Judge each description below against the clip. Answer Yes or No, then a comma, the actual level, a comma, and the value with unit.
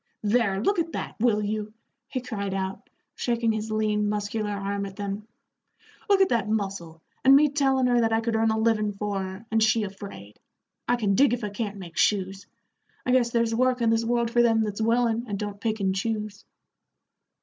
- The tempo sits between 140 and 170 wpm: No, fast, 205 wpm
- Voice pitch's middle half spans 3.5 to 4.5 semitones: No, narrow, 2.6 semitones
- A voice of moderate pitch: No, high, 220 Hz